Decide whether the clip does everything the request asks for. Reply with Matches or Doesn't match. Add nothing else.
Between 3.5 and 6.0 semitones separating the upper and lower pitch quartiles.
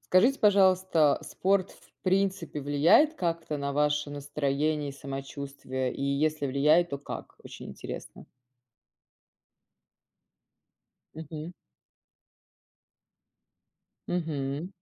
Matches